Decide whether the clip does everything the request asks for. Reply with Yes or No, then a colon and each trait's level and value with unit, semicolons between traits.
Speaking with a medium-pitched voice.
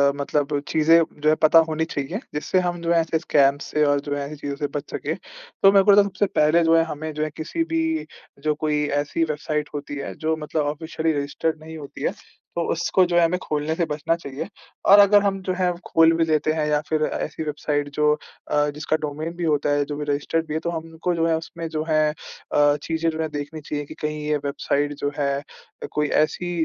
Yes: medium, 155 Hz